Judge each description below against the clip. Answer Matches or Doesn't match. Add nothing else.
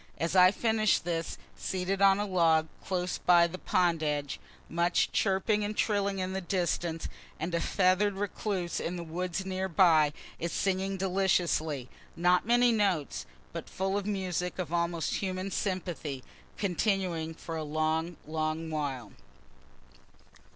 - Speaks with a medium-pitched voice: Matches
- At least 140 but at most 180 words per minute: Matches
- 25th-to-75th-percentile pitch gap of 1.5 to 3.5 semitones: Matches